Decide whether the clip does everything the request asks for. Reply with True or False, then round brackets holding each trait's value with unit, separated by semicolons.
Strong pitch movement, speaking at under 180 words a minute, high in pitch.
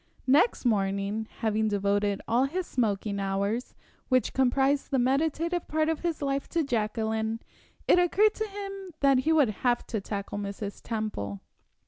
True (6.9 semitones; 150 wpm; 245 Hz)